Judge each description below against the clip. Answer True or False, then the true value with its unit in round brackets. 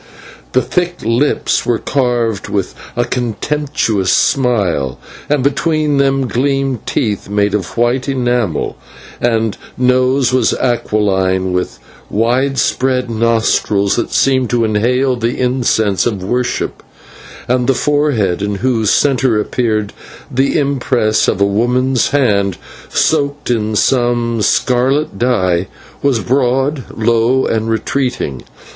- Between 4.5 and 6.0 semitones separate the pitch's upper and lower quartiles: False (3.7 semitones)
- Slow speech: True (115 wpm)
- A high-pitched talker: False (120 Hz)